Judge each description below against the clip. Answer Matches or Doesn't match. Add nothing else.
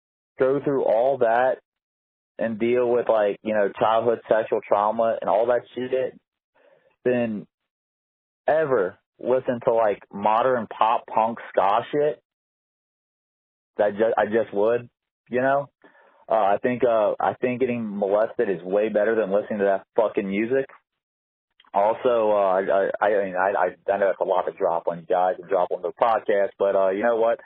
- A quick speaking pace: Doesn't match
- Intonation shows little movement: Doesn't match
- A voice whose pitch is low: Matches